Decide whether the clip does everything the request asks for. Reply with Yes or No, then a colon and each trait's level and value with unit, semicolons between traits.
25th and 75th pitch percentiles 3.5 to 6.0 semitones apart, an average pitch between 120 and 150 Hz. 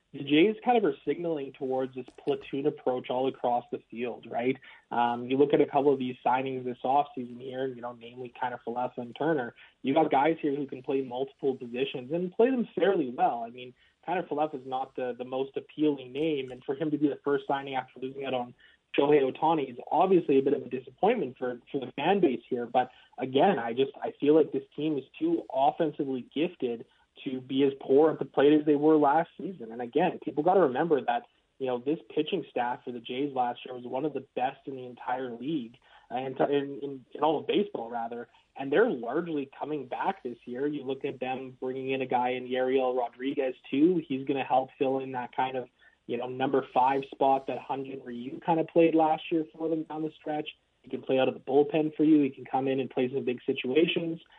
No: average, 2.9 semitones; low, 135 Hz